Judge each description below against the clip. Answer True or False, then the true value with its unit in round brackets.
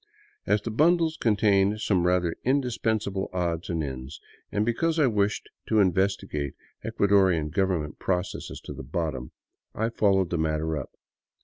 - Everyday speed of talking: True (145 wpm)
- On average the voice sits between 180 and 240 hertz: False (95 Hz)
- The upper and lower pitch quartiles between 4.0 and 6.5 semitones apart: True (4.7 semitones)